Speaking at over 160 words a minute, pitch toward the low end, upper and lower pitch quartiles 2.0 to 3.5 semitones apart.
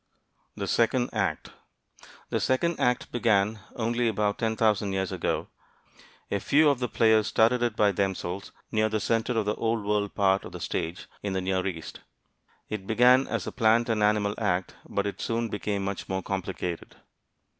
Yes: average, 175 wpm; low, 105 Hz; average, 2.9 semitones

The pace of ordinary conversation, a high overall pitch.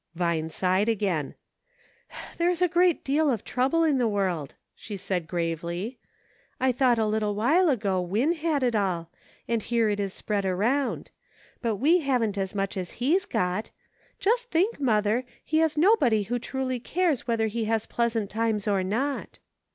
Yes: average, 175 wpm; high, 225 Hz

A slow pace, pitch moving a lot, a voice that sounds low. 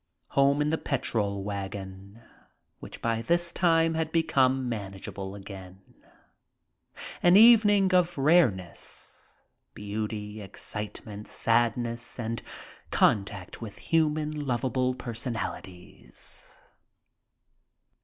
Yes: slow, 90 wpm; wide, 7.0 semitones; low, 115 Hz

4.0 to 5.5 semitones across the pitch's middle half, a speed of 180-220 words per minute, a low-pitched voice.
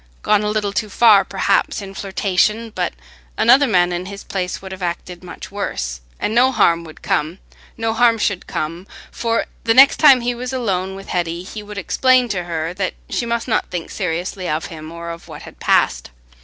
No: average, 4.4 semitones; average, 195 wpm; high, 195 Hz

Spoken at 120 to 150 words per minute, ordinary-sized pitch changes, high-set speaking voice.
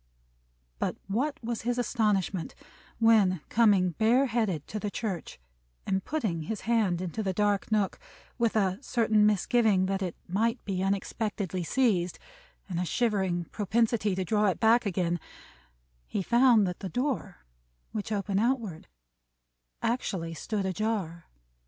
Yes: average, 140 wpm; average, 3.5 semitones; high, 205 Hz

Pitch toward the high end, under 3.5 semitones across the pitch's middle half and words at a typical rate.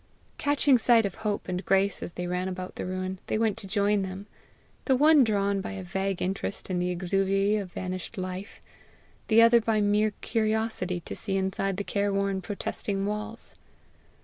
Yes: high, 195 Hz; narrow, 2.5 semitones; average, 180 wpm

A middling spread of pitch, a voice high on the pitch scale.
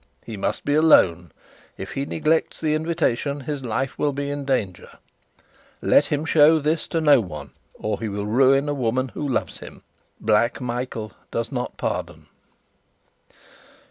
No: average, 4.5 semitones; low, 135 Hz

